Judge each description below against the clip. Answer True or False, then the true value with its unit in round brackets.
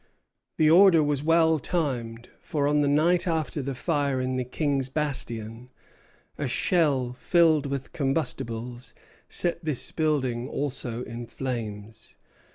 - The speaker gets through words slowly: True (130 wpm)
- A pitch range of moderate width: True (4.1 semitones)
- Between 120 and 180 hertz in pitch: True (140 Hz)